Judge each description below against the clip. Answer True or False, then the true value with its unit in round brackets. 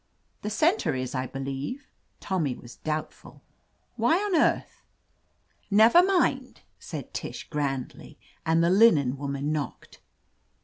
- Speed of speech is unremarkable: False (120 wpm)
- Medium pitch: True (155 Hz)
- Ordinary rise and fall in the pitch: False (8.9 semitones)